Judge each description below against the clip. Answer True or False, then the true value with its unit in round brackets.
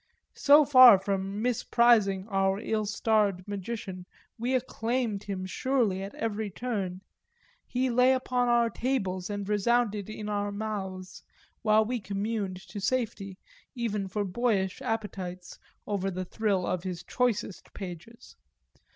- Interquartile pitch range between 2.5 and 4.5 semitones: True (3.5 semitones)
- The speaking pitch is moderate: False (210 Hz)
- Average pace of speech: False (130 wpm)